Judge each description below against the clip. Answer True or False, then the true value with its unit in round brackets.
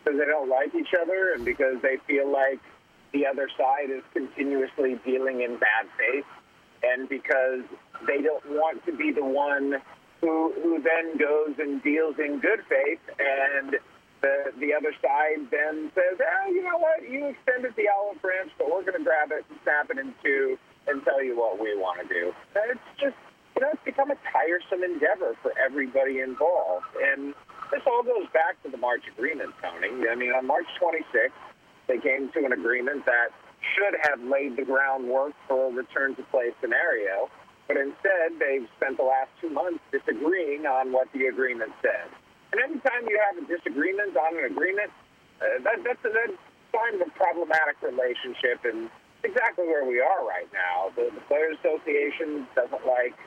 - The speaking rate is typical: True (185 wpm)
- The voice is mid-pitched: True (155 Hz)